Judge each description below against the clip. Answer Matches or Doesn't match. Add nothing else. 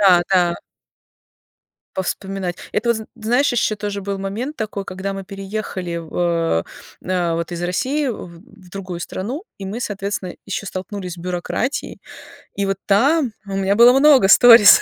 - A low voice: Doesn't match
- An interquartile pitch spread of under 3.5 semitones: Matches